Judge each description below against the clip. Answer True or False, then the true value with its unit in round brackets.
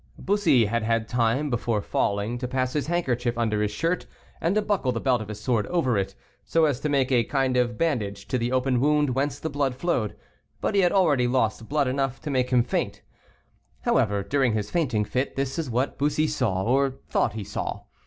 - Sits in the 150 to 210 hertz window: False (130 Hz)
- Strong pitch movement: False (4.0 semitones)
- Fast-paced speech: True (215 wpm)